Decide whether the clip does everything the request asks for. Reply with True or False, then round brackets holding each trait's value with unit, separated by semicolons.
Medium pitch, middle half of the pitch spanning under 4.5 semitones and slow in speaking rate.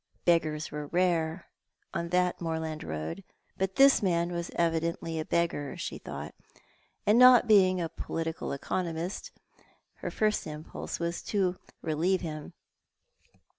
True (170 Hz; 2.5 semitones; 130 wpm)